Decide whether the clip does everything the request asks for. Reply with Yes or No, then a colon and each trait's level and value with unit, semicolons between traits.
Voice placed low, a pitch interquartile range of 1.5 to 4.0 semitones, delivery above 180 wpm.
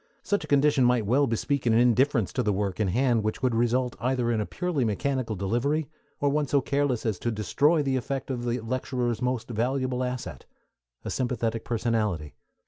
Yes: low, 125 Hz; average, 3.1 semitones; average, 190 wpm